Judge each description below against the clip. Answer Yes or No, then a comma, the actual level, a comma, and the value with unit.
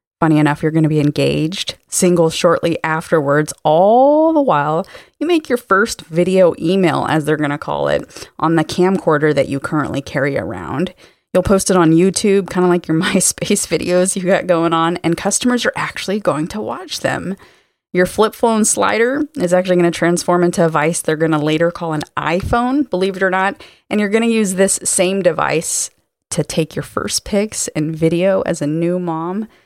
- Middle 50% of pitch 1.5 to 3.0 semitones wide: No, average, 3.5 semitones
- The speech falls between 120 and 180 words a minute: No, average, 200 wpm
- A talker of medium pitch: Yes, medium, 175 Hz